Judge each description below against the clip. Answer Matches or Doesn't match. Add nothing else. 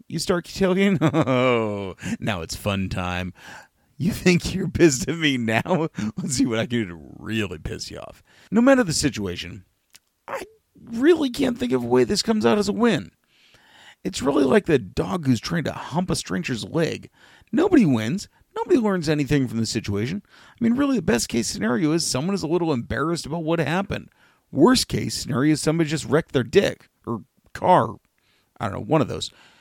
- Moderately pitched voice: Matches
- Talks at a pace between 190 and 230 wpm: Matches